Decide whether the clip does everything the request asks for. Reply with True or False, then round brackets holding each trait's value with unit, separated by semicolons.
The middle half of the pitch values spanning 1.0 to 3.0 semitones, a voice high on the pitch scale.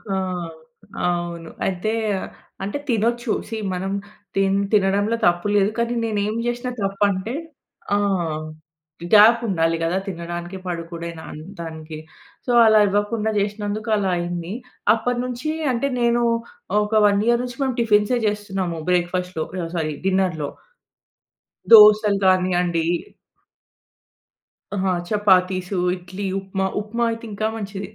False (3.6 semitones; 195 Hz)